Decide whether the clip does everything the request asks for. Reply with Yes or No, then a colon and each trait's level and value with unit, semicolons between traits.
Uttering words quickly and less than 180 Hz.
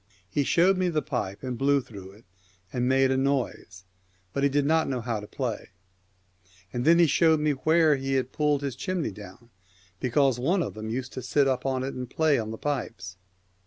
Yes: fast, 210 wpm; low, 135 Hz